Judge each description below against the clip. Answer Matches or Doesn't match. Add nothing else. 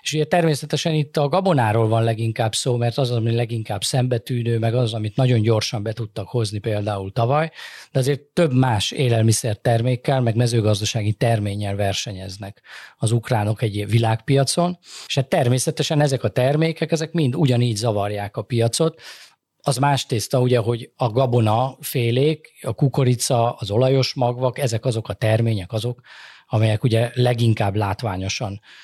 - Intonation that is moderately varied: Matches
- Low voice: Matches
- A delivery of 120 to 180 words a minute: Matches